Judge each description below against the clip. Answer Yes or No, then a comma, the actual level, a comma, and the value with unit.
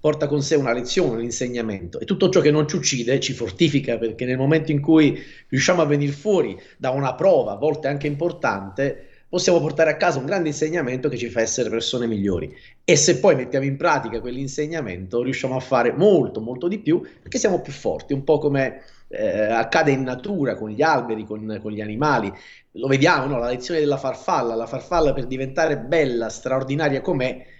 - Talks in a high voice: No, low, 135 Hz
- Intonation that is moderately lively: Yes, average, 4.3 semitones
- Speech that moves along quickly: Yes, fast, 200 wpm